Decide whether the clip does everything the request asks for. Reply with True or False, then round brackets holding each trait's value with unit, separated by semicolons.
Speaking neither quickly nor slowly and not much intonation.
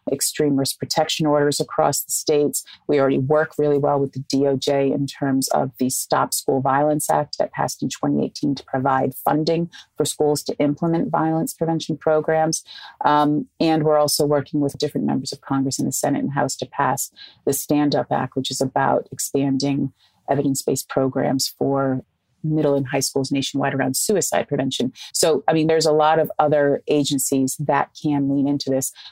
True (180 wpm; 2.0 semitones)